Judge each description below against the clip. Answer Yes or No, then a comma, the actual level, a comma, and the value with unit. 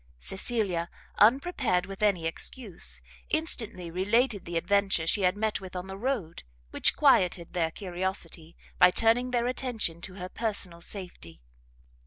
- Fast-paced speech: No, average, 140 wpm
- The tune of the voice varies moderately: Yes, average, 4.4 semitones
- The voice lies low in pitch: No, high, 190 Hz